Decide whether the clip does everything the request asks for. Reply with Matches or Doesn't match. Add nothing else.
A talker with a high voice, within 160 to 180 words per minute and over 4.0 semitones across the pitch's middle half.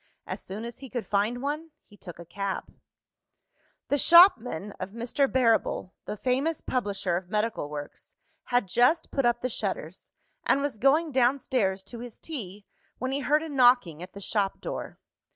Matches